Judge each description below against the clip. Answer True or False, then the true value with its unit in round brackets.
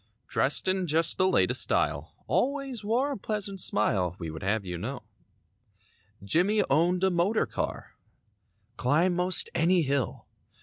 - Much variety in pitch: True (7.1 semitones)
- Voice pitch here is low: False (175 Hz)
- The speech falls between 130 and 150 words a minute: True (140 wpm)